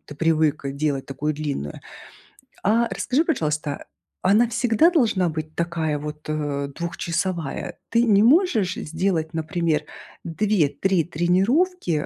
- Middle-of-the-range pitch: Yes, medium, 170 Hz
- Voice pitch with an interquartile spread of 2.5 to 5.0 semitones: No, wide, 5.6 semitones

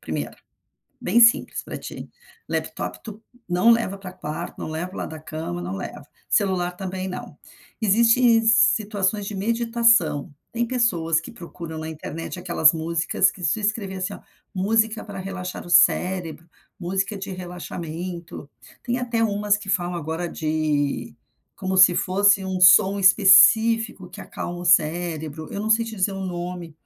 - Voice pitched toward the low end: No, medium, 185 Hz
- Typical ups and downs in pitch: Yes, average, 3.7 semitones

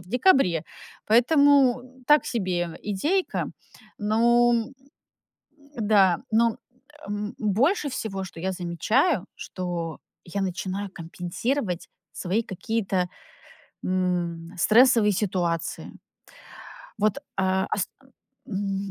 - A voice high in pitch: Yes, high, 200 Hz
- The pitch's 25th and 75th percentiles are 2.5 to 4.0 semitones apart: No, average, 4.6 semitones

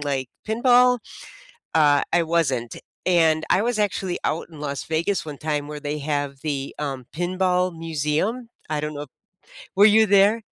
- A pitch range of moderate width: Yes, average, 4.9 semitones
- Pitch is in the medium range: Yes, medium, 160 Hz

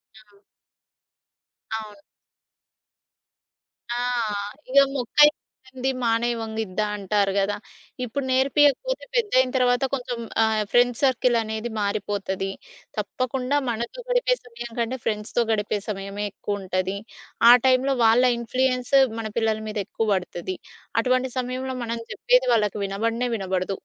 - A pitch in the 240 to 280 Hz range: No, high, 230 Hz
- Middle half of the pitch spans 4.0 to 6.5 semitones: No, average, 3.6 semitones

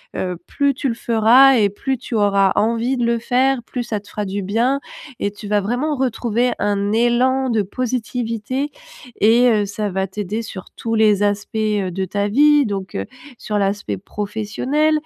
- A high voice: Yes, high, 220 Hz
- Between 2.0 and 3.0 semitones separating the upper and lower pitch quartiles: No, average, 3.6 semitones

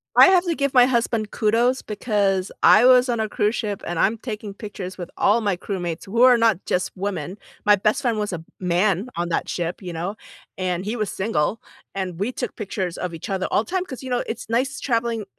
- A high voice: Yes, high, 210 Hz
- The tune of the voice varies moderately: Yes, average, 4.1 semitones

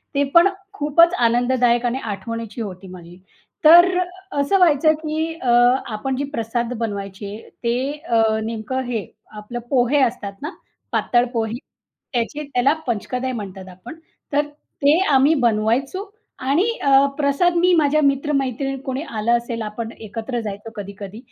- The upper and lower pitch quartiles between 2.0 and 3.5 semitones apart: No, average, 4.3 semitones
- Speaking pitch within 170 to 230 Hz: No, high, 245 Hz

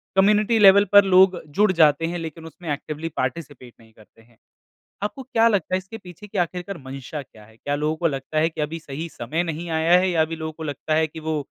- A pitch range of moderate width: Yes, average, 3.9 semitones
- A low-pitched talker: No, medium, 165 Hz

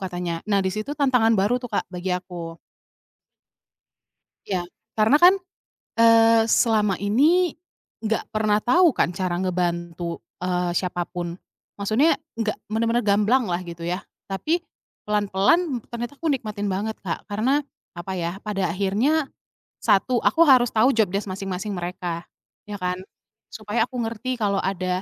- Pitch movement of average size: Yes, average, 3.8 semitones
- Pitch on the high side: Yes, high, 205 Hz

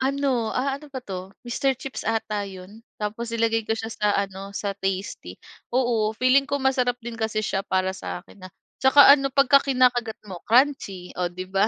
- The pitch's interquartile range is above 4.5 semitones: Yes, average, 4.9 semitones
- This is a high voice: Yes, high, 225 Hz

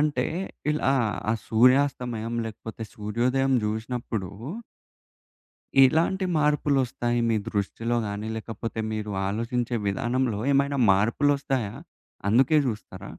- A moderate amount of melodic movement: Yes, average, 3.6 semitones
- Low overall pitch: Yes, low, 120 Hz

